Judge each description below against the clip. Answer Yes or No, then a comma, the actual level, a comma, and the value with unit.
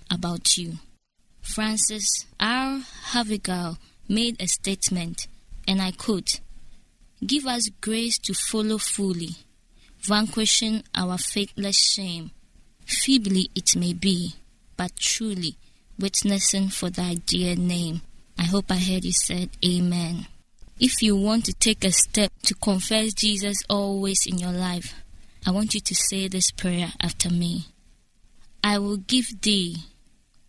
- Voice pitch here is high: Yes, high, 195 Hz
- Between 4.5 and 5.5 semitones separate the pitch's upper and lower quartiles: No, average, 3.3 semitones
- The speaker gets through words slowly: Yes, slow, 130 wpm